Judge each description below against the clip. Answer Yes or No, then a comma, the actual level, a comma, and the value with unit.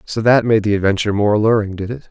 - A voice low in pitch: Yes, low, 105 Hz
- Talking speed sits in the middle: No, fast, 255 wpm